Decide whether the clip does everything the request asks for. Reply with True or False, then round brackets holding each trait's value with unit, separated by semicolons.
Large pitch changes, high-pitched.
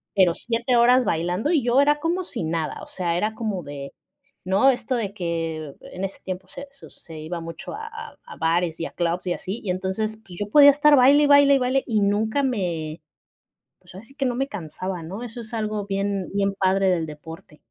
True (6.2 semitones; 200 Hz)